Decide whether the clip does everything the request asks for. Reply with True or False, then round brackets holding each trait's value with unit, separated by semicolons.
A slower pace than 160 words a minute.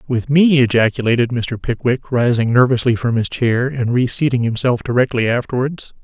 True (150 wpm)